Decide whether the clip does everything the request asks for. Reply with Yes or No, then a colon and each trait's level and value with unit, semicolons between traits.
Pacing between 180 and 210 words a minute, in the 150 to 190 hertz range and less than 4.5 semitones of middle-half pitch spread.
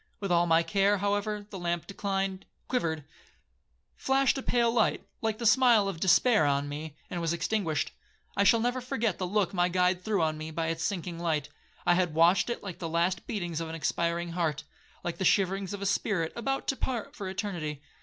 Yes: average, 195 wpm; medium, 185 Hz; average, 3.8 semitones